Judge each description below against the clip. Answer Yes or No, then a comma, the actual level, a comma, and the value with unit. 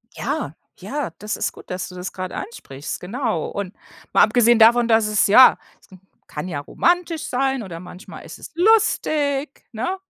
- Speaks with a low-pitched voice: No, high, 230 Hz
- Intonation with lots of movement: Yes, wide, 7.3 semitones